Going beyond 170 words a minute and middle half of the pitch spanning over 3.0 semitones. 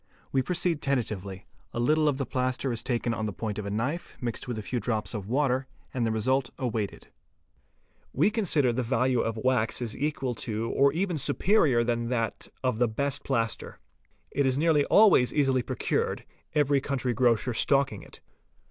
Yes: average, 185 wpm; average, 3.6 semitones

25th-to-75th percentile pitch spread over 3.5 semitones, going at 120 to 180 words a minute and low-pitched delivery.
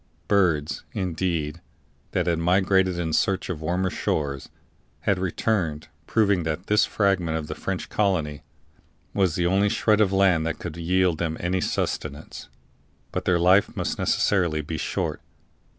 No: average, 3.1 semitones; average, 150 wpm; very low, 90 Hz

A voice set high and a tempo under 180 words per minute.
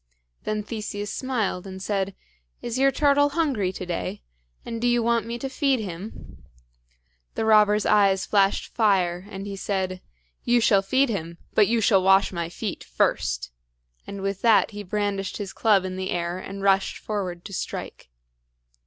Yes: high, 200 Hz; average, 170 wpm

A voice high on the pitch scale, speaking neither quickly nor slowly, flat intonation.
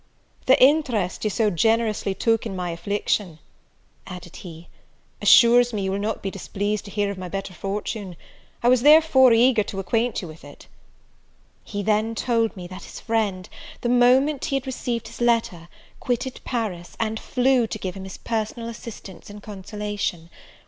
No: high, 215 Hz; average, 170 wpm; average, 3.7 semitones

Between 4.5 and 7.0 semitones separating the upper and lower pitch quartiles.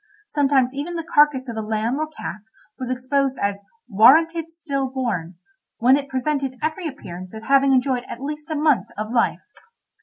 No: average, 4.0 semitones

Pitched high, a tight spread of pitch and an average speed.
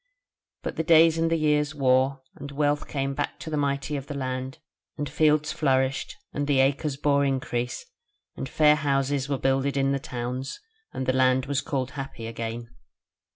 No: medium, 140 Hz; narrow, 1.9 semitones; average, 180 wpm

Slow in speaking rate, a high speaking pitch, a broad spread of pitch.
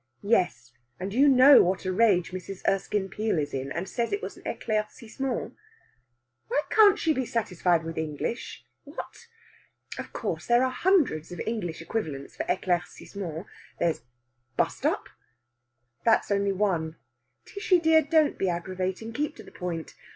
No: average, 150 wpm; high, 200 Hz; wide, 6.6 semitones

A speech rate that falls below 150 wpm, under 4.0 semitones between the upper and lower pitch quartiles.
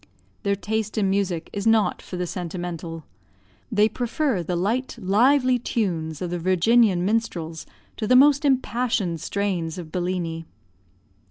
No: average, 140 wpm; average, 4.7 semitones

